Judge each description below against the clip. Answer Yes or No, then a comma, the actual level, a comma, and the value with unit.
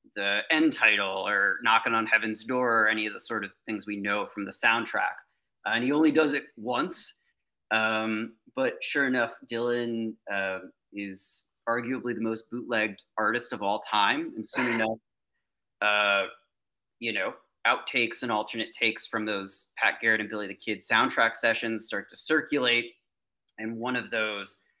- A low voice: Yes, low, 110 Hz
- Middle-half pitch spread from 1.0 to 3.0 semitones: Yes, narrow, 2.5 semitones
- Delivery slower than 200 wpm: Yes, average, 165 wpm